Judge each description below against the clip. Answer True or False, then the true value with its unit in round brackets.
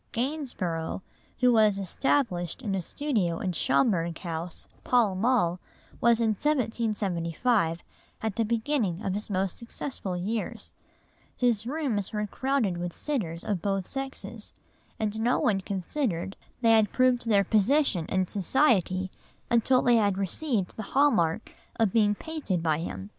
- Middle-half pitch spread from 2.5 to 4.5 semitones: False (5.0 semitones)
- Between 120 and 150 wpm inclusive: True (140 wpm)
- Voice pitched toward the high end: True (210 Hz)